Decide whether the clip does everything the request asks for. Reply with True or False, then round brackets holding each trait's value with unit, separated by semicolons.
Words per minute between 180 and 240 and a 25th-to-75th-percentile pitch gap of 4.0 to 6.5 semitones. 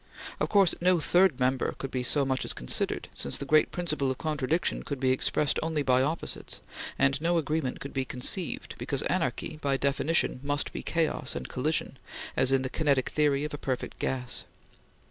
False (185 wpm; 3.0 semitones)